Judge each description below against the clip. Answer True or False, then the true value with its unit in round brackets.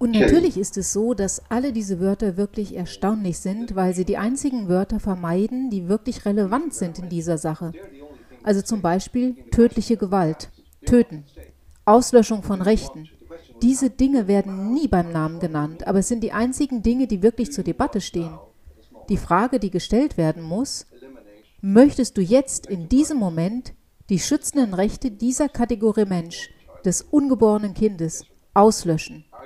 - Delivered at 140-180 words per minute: True (150 wpm)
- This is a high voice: True (205 Hz)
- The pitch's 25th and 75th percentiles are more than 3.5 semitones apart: True (5.2 semitones)